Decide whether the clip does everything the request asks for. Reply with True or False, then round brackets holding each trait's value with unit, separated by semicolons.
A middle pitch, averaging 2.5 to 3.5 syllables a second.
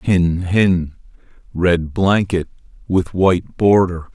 False (90 Hz; 3.3 syllables/s)